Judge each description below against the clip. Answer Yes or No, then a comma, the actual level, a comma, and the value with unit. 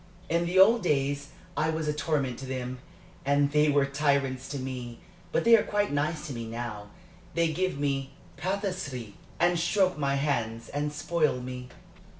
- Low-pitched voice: No, medium, 145 Hz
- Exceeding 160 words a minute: Yes, average, 170 wpm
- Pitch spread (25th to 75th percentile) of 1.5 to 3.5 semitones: No, average, 4.1 semitones